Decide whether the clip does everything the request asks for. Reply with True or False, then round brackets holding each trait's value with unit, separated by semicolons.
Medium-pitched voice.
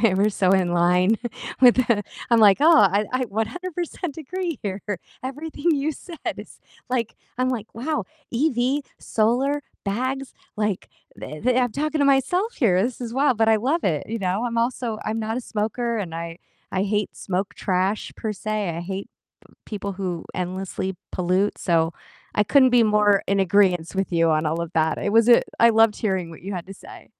False (215 Hz)